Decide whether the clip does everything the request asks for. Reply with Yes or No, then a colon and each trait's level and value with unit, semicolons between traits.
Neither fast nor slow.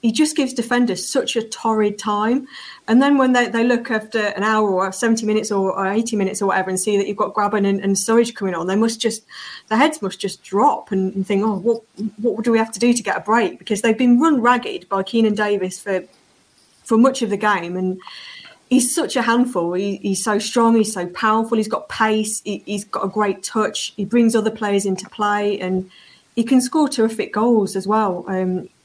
No: fast, 230 wpm